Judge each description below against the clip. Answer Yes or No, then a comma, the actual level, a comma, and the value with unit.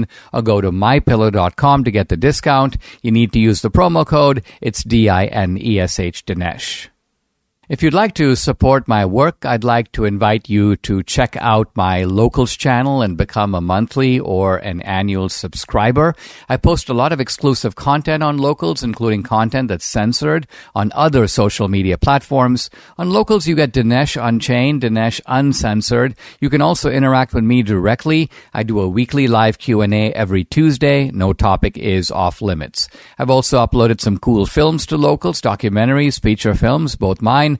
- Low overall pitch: Yes, low, 115 Hz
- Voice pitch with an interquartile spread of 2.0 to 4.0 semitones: No, average, 5.1 semitones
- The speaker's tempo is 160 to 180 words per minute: Yes, average, 175 wpm